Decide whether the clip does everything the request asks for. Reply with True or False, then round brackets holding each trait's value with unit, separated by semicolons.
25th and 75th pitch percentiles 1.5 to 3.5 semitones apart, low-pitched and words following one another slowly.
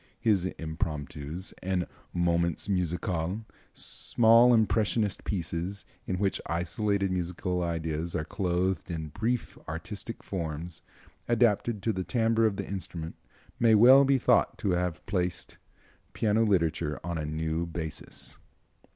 False (4.2 semitones; 90 Hz; 125 wpm)